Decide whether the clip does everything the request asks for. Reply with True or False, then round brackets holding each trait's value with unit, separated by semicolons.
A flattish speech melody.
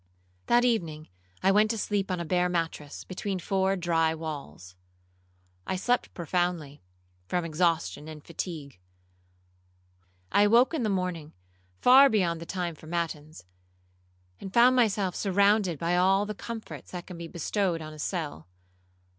False (3.8 semitones)